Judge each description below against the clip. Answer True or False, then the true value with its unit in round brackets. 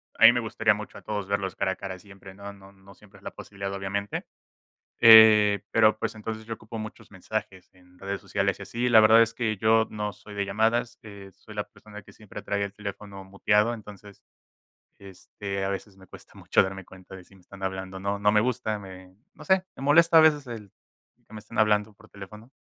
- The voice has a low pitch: True (105 Hz)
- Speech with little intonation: True (2.0 semitones)